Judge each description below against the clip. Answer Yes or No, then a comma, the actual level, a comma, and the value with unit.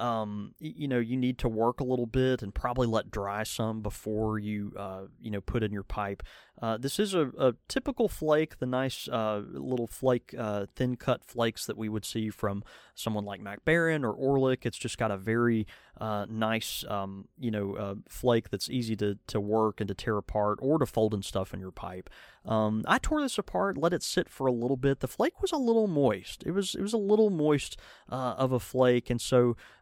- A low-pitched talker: Yes, low, 115 Hz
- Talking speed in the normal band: No, fast, 225 wpm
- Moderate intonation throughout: Yes, average, 4.0 semitones